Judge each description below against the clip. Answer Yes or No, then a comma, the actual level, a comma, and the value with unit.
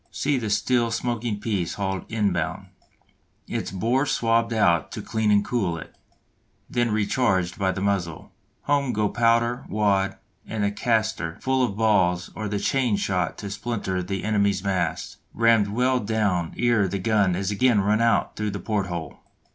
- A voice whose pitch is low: Yes, low, 105 Hz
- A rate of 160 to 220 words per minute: Yes, average, 165 wpm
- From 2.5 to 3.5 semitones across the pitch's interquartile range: Yes, average, 3.2 semitones